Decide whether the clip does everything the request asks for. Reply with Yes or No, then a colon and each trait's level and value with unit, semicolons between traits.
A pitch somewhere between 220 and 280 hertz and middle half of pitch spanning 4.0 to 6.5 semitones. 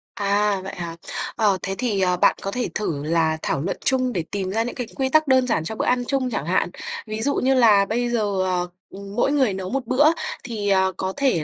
No: high, 205 Hz; average, 4.9 semitones